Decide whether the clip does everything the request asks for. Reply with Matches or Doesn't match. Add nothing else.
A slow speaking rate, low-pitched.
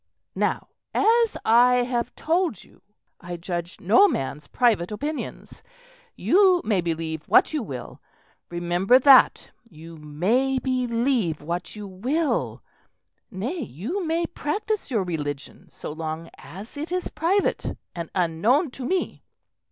Doesn't match